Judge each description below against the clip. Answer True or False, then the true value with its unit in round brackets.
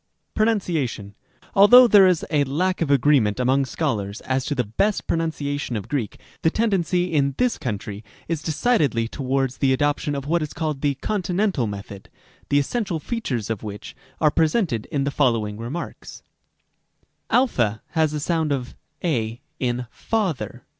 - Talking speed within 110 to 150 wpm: False (170 wpm)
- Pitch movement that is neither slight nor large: False (6.0 semitones)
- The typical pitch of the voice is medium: True (145 Hz)